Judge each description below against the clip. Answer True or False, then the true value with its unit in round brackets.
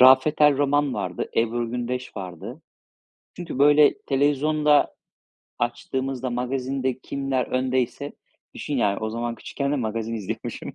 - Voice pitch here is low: True (130 Hz)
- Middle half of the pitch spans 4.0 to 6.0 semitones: False (3.0 semitones)